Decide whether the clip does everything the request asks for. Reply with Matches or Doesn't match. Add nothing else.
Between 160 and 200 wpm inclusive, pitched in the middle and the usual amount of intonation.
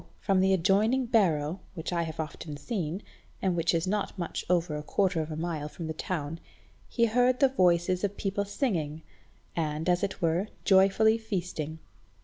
Matches